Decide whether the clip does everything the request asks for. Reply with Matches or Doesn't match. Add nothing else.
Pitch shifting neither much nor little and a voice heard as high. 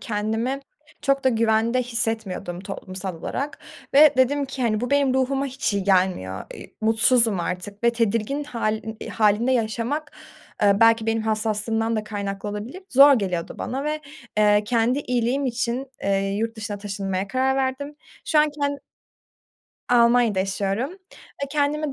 Matches